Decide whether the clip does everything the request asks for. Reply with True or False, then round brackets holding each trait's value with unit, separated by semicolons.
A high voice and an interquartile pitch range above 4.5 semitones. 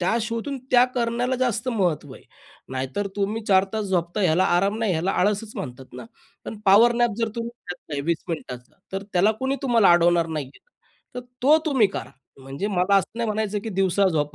True (200 Hz; 4.9 semitones)